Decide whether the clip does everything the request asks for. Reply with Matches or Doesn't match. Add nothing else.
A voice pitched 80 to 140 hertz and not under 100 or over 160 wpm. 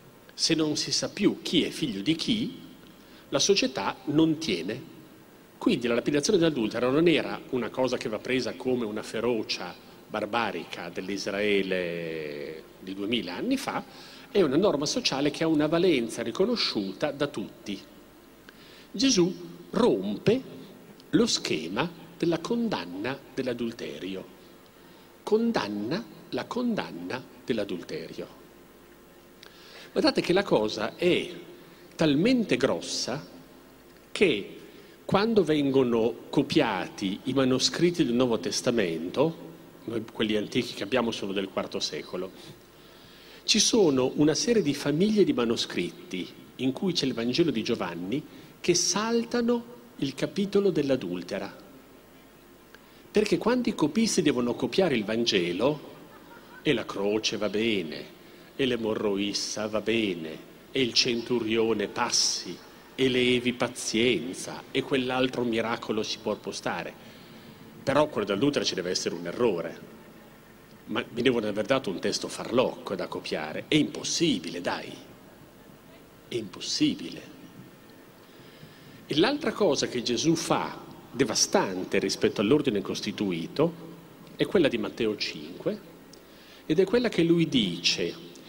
Matches